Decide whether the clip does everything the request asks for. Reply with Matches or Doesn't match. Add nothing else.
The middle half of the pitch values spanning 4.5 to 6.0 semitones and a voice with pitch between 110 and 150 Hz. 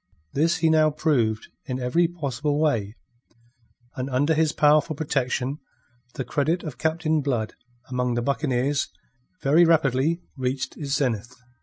Doesn't match